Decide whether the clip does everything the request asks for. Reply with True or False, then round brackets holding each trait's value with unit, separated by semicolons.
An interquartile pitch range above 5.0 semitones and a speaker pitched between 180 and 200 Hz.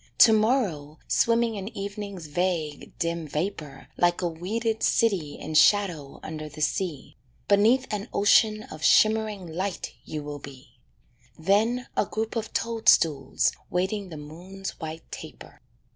True (5.5 semitones; 185 Hz)